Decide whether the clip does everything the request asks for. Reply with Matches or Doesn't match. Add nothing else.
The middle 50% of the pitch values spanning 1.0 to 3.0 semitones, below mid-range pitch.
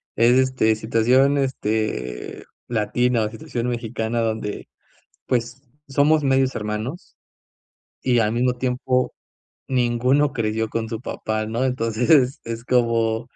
Matches